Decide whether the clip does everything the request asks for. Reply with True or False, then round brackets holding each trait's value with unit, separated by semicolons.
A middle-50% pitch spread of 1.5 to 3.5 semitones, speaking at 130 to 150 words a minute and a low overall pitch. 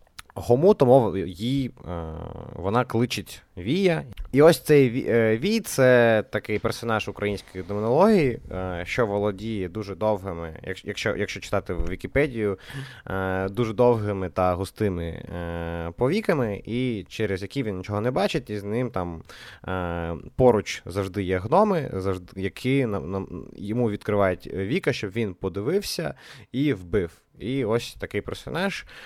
False (4.8 semitones; 135 wpm; 105 Hz)